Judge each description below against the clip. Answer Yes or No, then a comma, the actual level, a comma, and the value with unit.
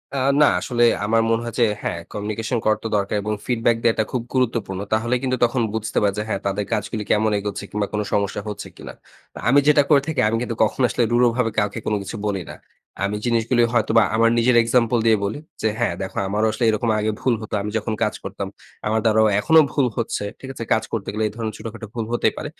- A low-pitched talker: Yes, low, 110 Hz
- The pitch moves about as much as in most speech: No, narrow, 2.2 semitones